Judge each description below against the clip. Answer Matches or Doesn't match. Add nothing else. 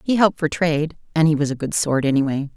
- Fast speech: Matches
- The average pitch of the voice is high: Doesn't match